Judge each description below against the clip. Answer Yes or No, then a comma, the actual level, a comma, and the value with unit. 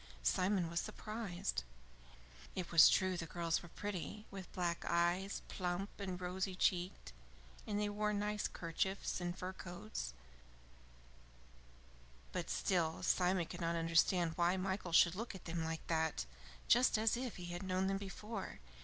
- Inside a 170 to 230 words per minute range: No, average, 150 wpm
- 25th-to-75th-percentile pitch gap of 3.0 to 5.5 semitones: No, narrow, 2.6 semitones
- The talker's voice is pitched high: No, medium, 180 Hz